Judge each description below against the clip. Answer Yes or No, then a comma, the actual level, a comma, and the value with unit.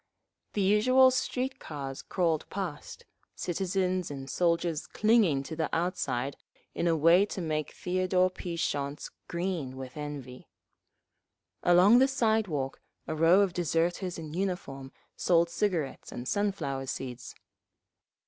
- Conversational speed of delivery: No, slow, 125 wpm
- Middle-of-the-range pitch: Yes, medium, 170 Hz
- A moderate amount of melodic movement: Yes, average, 4.6 semitones